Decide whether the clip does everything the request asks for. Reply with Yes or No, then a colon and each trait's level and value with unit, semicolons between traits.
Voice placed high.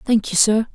Yes: high, 215 Hz